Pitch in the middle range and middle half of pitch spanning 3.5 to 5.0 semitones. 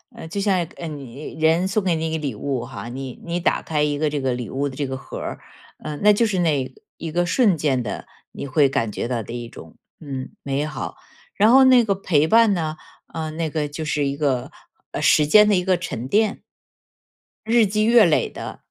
No: medium, 155 Hz; wide, 5.6 semitones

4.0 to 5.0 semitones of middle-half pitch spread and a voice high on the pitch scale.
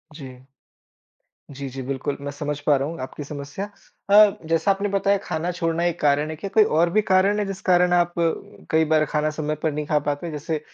No: average, 4.3 semitones; medium, 160 Hz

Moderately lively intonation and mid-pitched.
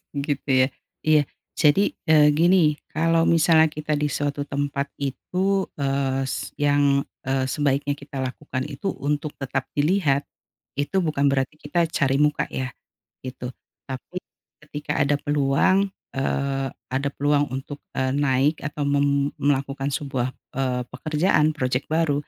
No: narrow, 2.0 semitones; medium, 145 Hz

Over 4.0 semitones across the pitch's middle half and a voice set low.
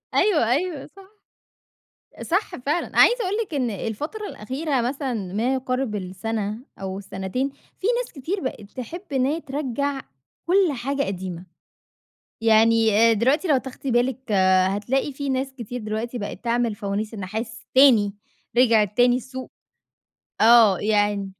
No: average, 4.6 semitones; high, 245 Hz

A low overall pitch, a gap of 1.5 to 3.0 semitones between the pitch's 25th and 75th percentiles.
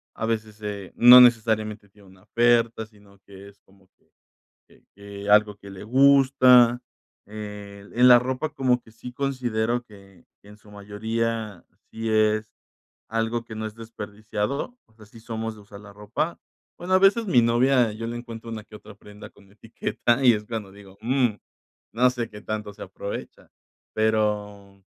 Yes: low, 110 Hz; narrow, 2.5 semitones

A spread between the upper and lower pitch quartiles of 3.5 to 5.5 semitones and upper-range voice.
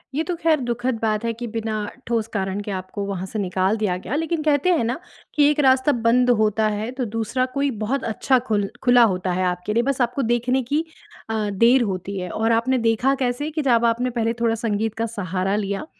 Yes: average, 3.8 semitones; high, 230 Hz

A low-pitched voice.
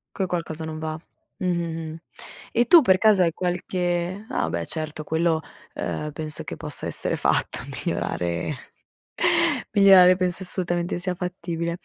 No: medium, 175 Hz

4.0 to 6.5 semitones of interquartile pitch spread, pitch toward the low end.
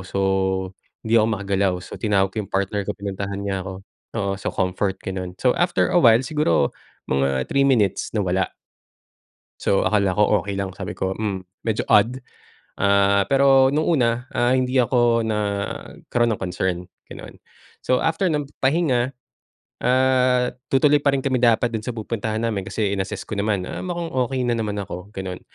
Yes: average, 4.5 semitones; low, 110 Hz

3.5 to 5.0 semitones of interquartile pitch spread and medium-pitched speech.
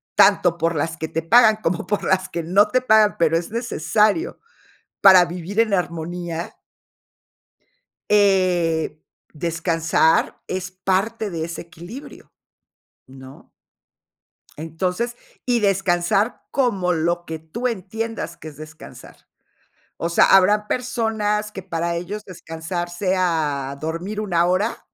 Yes: average, 4.0 semitones; medium, 180 Hz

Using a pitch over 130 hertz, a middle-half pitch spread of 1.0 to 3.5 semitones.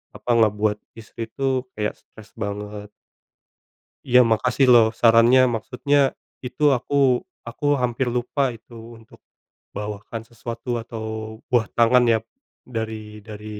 No: low, 115 Hz; narrow, 2.5 semitones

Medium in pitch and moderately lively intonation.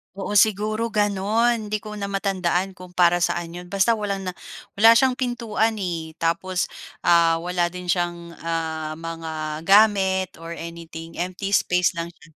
Yes: medium, 180 Hz; average, 3.6 semitones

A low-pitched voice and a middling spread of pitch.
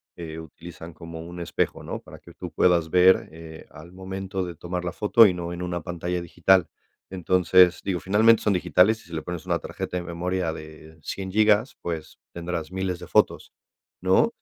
No: very low, 90 Hz; narrow, 1.9 semitones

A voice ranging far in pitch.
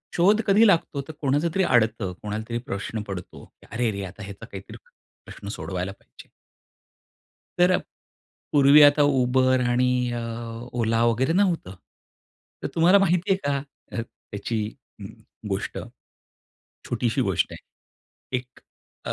Yes: wide, 7.3 semitones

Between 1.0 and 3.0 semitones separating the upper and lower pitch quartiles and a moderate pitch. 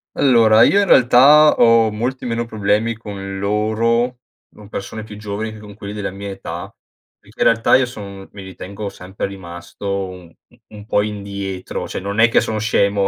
No: narrow, 2.6 semitones; low, 105 Hz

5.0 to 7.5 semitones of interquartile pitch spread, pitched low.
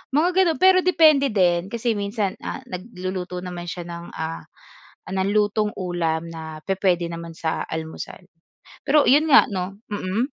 No: average, 5.3 semitones; medium, 185 Hz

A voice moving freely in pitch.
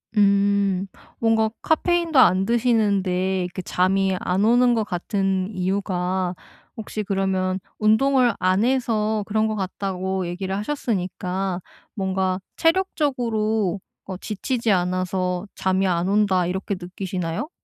No: average, 2.9 semitones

